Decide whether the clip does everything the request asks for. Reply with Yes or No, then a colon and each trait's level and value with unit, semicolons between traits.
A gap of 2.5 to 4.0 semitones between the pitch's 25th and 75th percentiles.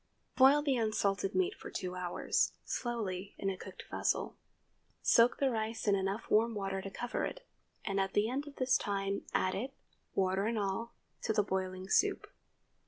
Yes: average, 3.7 semitones